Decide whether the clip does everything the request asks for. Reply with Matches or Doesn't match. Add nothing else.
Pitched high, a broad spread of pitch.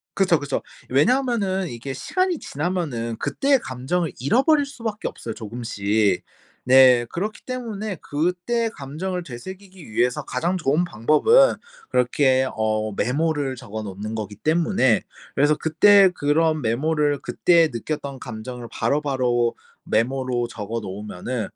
Doesn't match